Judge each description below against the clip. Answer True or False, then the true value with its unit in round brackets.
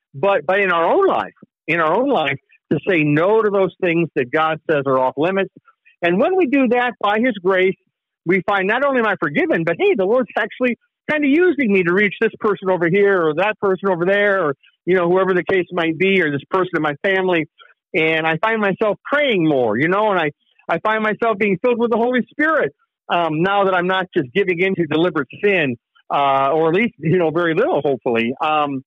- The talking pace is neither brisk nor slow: False (230 wpm)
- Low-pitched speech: False (190 Hz)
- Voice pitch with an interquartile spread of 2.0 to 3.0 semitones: False (4.5 semitones)